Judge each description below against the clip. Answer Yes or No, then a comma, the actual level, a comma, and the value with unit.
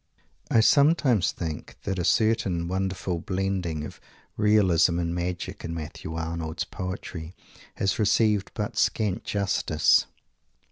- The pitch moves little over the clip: No, average, 3.6 semitones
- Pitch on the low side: Yes, very low, 95 Hz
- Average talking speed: No, slow, 120 wpm